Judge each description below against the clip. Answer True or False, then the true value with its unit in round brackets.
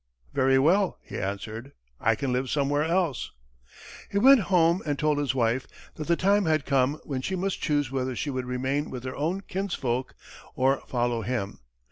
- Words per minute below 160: False (180 wpm)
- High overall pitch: False (140 Hz)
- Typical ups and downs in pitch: True (4.7 semitones)